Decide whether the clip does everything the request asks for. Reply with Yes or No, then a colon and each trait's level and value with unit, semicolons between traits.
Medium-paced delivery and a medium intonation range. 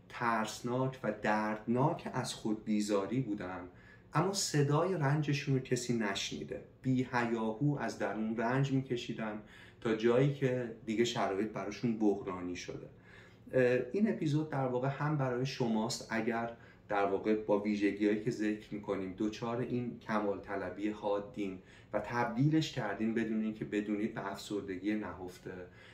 Yes: average, 130 wpm; average, 3.5 semitones